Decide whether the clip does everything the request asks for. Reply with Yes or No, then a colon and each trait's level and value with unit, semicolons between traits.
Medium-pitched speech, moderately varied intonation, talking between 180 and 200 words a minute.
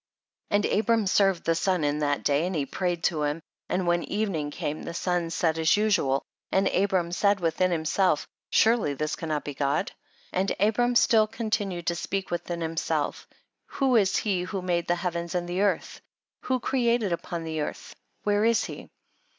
Yes: medium, 180 Hz; average, 3.9 semitones; average, 185 wpm